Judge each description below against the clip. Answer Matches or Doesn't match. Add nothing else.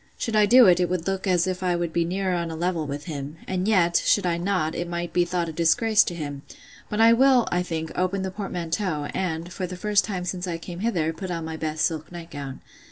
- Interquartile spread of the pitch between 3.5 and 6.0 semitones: Doesn't match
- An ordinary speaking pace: Doesn't match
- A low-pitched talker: Doesn't match